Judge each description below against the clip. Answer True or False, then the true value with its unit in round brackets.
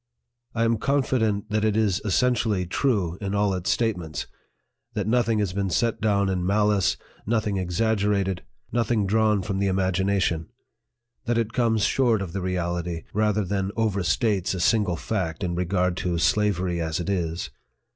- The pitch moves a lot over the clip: False (3.1 semitones)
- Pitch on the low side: True (100 Hz)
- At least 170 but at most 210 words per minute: False (160 wpm)